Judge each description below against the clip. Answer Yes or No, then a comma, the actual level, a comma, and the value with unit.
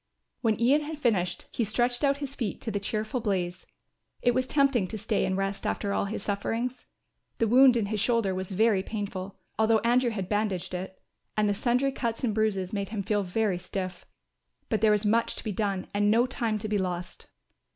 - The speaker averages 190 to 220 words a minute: Yes, fast, 205 wpm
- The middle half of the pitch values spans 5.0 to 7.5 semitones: No, average, 3.3 semitones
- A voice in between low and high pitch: No, high, 215 Hz